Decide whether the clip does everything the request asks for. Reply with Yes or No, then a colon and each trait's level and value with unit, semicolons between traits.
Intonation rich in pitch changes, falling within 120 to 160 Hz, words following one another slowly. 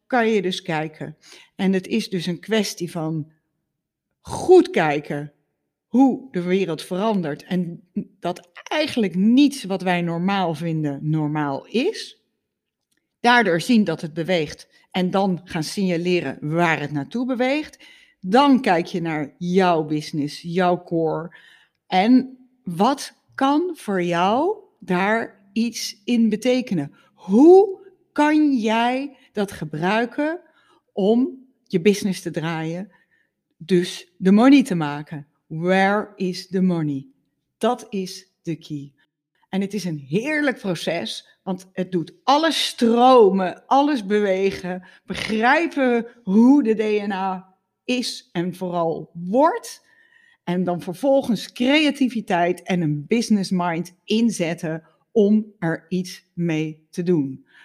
No: wide, 6.0 semitones; high, 190 Hz; slow, 120 wpm